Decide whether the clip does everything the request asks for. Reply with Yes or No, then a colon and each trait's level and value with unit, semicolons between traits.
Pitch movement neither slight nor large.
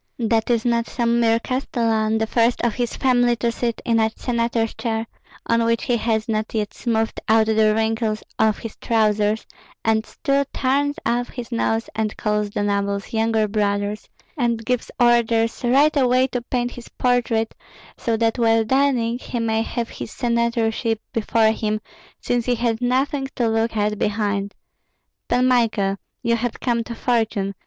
No: narrow, 1.7 semitones